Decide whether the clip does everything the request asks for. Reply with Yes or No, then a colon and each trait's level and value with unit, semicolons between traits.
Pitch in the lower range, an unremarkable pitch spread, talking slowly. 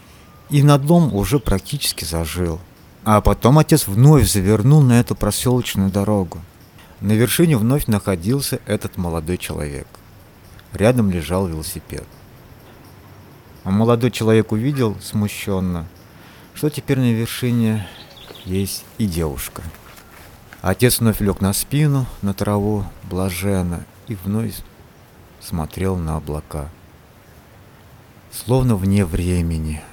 Yes: low, 100 Hz; average, 4.6 semitones; slow, 105 wpm